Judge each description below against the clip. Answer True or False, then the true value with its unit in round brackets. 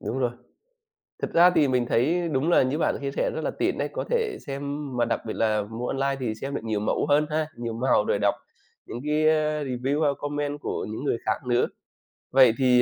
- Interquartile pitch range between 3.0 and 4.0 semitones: True (3.7 semitones)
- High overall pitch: False (130 Hz)